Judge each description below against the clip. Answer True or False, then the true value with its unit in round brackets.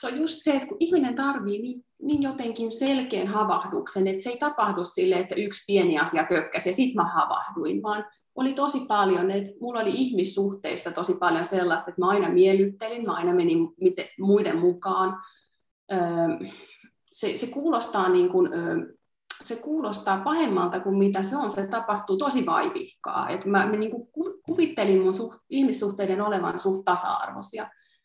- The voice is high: True (215 Hz)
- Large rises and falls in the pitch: True (6.9 semitones)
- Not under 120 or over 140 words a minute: False (155 wpm)